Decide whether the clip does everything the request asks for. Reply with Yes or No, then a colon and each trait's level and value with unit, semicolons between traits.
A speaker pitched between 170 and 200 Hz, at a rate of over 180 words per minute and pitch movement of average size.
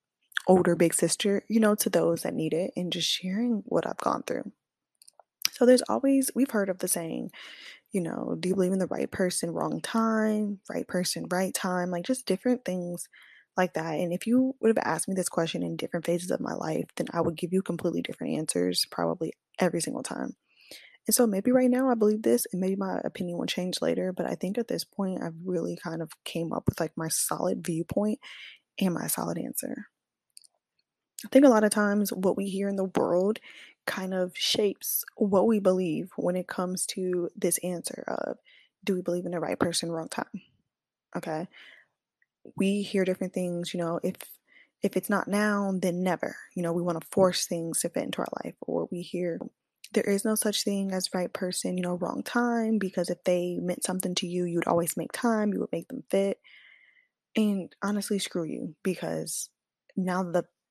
Yes: medium, 185 Hz; fast, 205 wpm; average, 3.2 semitones